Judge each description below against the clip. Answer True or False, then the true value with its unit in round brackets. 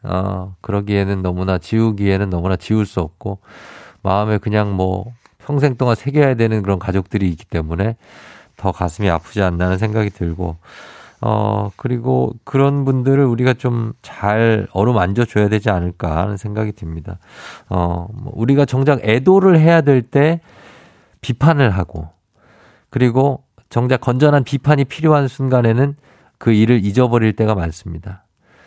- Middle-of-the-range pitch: False (110 Hz)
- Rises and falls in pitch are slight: False (5.3 semitones)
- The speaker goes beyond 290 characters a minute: True (305 characters per minute)